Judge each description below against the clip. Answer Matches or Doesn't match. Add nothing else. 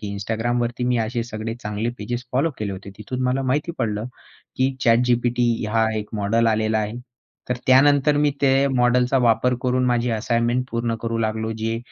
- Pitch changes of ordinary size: Doesn't match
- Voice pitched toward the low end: Matches